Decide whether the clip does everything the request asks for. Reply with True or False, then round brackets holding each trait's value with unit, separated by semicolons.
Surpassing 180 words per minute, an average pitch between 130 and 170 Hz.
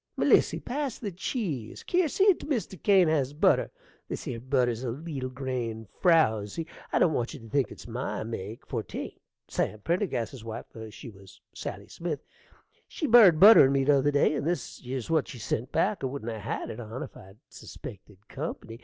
True (190 wpm; 135 Hz)